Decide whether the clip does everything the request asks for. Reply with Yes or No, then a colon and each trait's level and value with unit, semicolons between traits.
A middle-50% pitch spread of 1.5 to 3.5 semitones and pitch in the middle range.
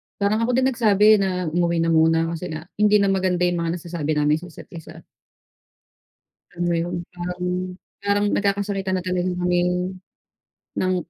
Yes: average, 2.9 semitones; medium, 180 Hz